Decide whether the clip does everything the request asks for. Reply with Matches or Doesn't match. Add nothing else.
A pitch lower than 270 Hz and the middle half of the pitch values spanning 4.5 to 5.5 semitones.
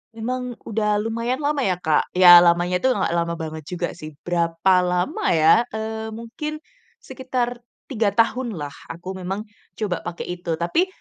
Matches